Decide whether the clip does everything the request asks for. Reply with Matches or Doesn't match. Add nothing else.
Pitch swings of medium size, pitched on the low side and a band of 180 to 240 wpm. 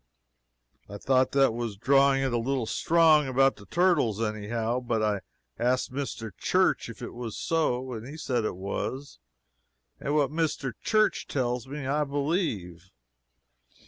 Doesn't match